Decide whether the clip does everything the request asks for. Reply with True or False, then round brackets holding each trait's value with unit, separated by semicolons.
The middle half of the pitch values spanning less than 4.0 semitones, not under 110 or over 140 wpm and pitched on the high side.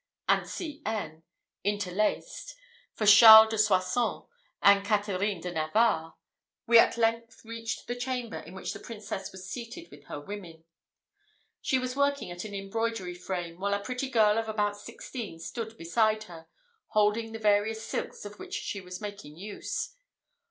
False (3.2 semitones; 160 wpm; 210 Hz)